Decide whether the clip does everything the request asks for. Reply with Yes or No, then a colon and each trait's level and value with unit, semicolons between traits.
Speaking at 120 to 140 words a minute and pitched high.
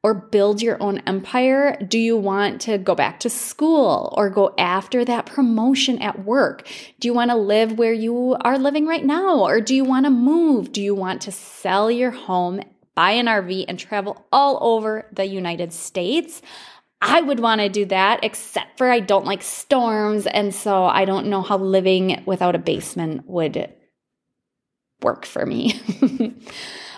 No: average, 180 wpm; high, 215 Hz